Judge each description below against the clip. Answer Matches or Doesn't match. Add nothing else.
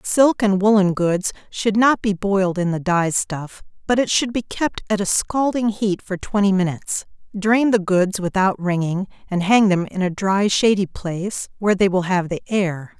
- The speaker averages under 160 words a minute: Doesn't match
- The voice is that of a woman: Matches